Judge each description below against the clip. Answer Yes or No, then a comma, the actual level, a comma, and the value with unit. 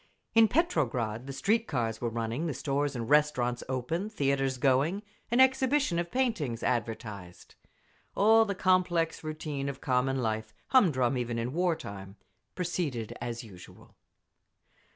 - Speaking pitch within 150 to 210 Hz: No, medium, 140 Hz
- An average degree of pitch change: No, wide, 7.0 semitones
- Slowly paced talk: Yes, slow, 130 wpm